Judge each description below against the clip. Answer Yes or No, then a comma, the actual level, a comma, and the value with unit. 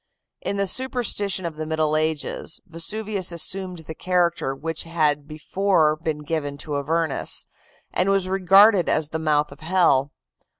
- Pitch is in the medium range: Yes, medium, 165 Hz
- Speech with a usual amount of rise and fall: Yes, average, 3.6 semitones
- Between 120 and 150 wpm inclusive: Yes, average, 145 wpm